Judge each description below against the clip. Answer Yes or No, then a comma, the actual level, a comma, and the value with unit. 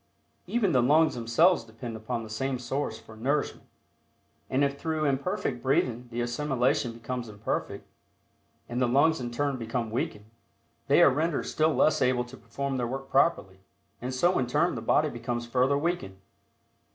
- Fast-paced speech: No, average, 165 wpm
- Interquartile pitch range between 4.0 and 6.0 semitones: No, average, 3.4 semitones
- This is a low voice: Yes, low, 130 Hz